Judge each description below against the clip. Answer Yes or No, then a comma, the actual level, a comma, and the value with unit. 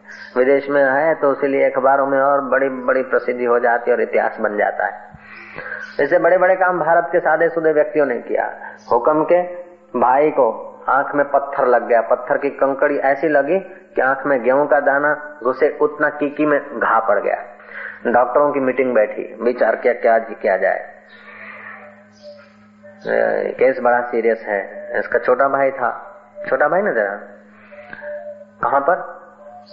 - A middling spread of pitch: Yes, average, 5.0 semitones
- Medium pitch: Yes, medium, 150 Hz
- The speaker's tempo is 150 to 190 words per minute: Yes, average, 155 wpm